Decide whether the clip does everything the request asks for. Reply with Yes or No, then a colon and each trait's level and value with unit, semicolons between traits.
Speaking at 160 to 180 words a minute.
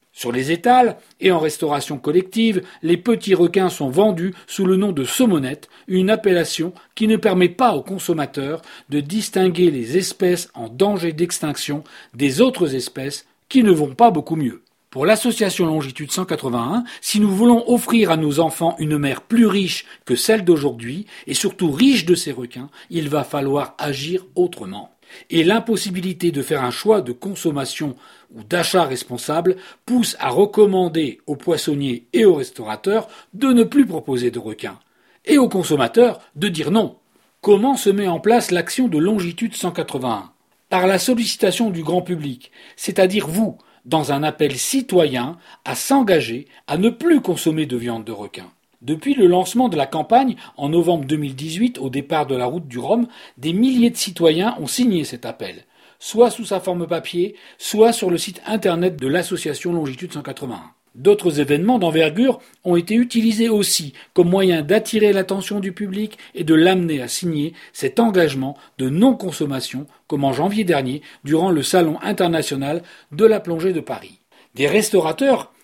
Yes: average, 165 wpm